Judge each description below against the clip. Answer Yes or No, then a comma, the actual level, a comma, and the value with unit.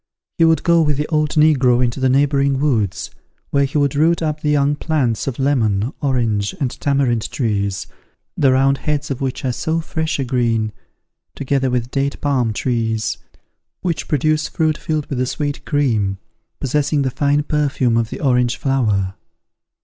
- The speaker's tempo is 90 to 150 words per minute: No, average, 170 wpm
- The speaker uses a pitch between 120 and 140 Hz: Yes, low, 135 Hz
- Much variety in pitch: No, average, 3.6 semitones